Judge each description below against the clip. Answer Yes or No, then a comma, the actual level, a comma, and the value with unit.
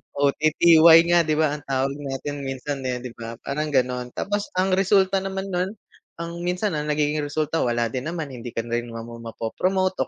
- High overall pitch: No, medium, 150 Hz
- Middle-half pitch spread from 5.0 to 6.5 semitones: Yes, wide, 5.6 semitones